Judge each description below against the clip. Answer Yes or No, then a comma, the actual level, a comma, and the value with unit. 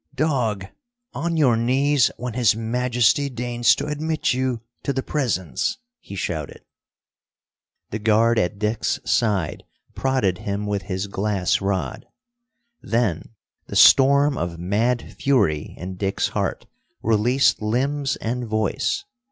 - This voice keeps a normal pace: No, slow, 125 wpm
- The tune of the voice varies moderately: Yes, average, 4.7 semitones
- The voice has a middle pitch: No, low, 115 Hz